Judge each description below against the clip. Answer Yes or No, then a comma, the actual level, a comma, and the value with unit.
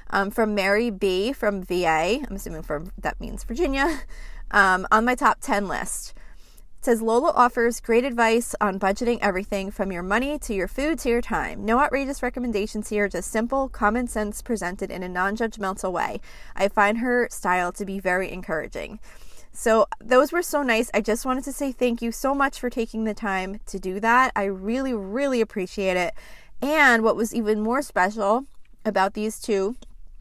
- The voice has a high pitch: Yes, high, 215 Hz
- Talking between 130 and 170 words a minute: No, average, 185 wpm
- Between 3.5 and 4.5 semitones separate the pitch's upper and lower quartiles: Yes, average, 3.8 semitones